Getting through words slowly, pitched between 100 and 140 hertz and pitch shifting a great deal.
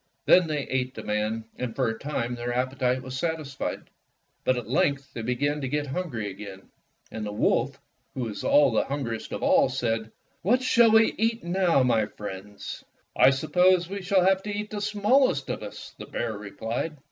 No: average, 195 wpm; low, 135 Hz; wide, 7.8 semitones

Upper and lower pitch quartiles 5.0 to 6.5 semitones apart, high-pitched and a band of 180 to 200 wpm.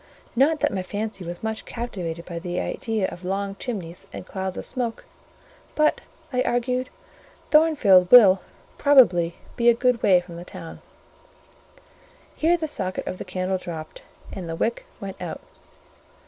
No: wide, 5.4 semitones; high, 195 Hz; average, 150 wpm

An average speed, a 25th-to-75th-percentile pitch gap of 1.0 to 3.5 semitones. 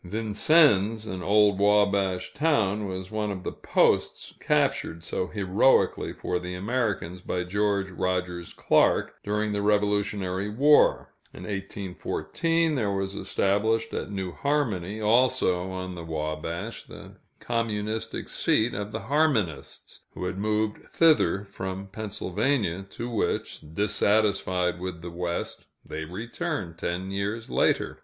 No: slow, 125 wpm; average, 3.0 semitones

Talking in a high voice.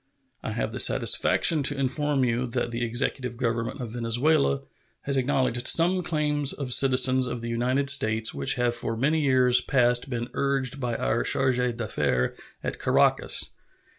No: low, 125 Hz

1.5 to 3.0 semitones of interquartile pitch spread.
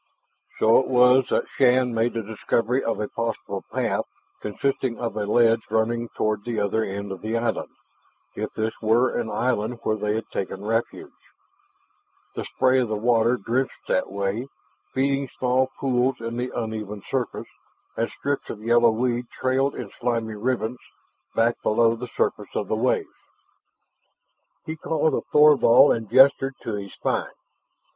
Yes: narrow, 2.5 semitones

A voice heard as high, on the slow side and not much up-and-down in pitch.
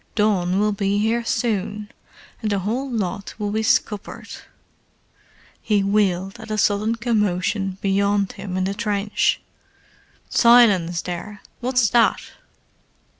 Yes: high, 205 Hz; slow, 125 wpm; narrow, 2.1 semitones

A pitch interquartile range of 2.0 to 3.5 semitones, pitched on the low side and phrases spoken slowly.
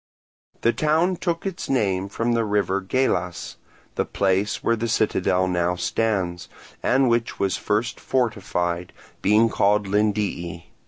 No: average, 4.0 semitones; low, 105 Hz; slow, 130 wpm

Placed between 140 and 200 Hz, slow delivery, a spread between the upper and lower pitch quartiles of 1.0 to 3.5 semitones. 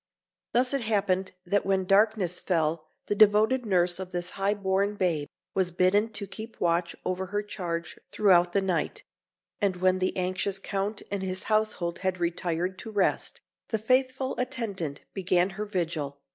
No: high, 190 Hz; average, 160 wpm; average, 2.7 semitones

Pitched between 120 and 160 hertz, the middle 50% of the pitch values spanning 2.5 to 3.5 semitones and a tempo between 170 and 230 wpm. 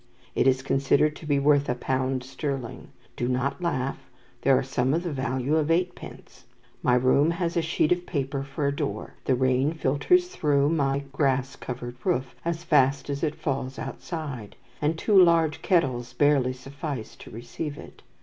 Yes: medium, 140 Hz; average, 3.2 semitones; average, 175 wpm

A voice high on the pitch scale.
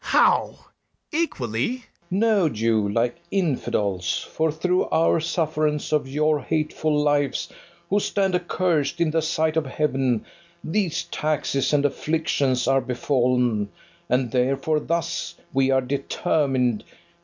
No: medium, 150 Hz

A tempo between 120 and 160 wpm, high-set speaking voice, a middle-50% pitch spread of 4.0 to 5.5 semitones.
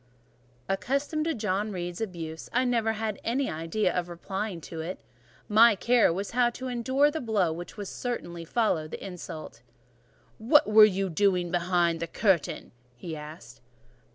Yes: average, 155 wpm; high, 195 Hz; average, 5.2 semitones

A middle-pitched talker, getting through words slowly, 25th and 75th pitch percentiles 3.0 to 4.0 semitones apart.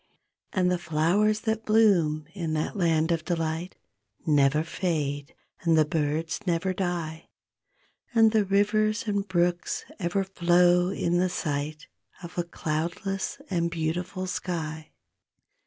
Yes: medium, 175 Hz; slow, 125 wpm; average, 3.3 semitones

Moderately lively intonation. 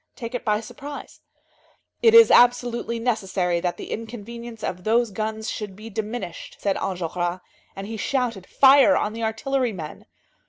Yes: average, 3.8 semitones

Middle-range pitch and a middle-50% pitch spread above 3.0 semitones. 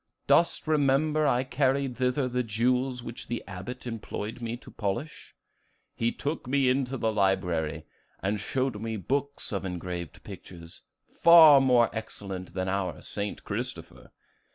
No: low, 120 Hz; wide, 5.5 semitones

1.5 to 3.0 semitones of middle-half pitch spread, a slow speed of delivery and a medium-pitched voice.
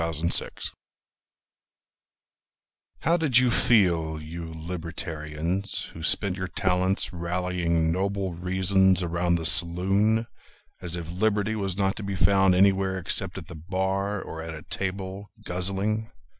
No: narrow, 2.6 semitones; slow, 130 wpm; very low, 90 Hz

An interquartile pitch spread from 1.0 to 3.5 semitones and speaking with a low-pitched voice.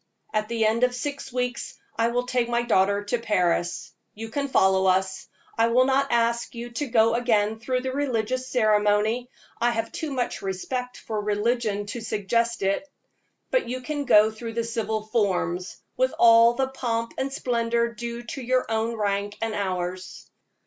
No: average, 2.9 semitones; high, 230 Hz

